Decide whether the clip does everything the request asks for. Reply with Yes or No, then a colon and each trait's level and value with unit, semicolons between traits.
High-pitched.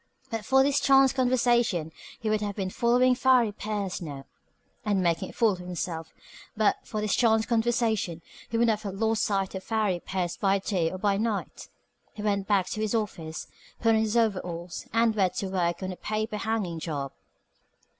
Yes: high, 210 Hz